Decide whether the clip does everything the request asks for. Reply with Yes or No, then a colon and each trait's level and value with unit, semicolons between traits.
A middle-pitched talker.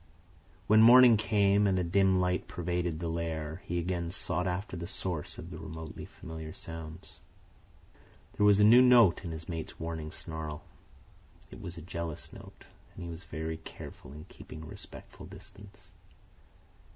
No: very low, 85 Hz